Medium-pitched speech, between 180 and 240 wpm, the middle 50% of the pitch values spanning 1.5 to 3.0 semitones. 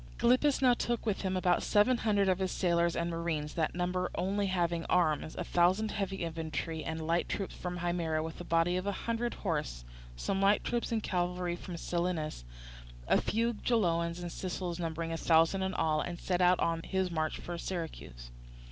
Yes: medium, 175 Hz; average, 190 wpm; narrow, 2.6 semitones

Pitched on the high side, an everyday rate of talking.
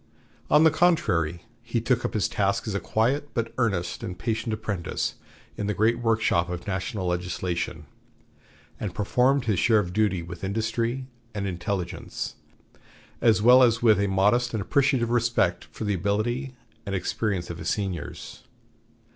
No: low, 105 Hz; average, 155 wpm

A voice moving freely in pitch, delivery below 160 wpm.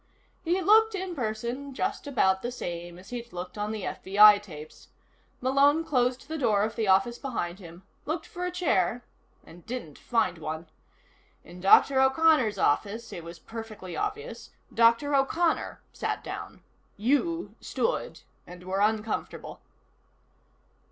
Yes: wide, 7.0 semitones; average, 140 wpm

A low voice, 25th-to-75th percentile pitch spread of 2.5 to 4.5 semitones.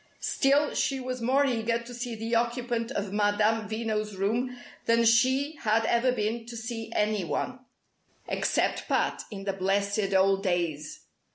No: high, 225 Hz; average, 3.0 semitones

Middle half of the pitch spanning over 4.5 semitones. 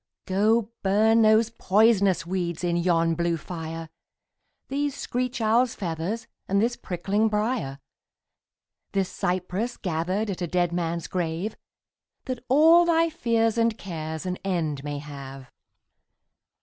Yes: average, 5.1 semitones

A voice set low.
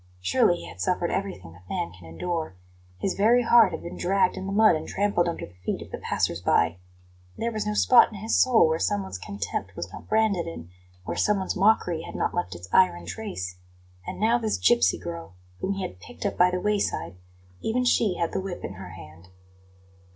No: medium, 180 Hz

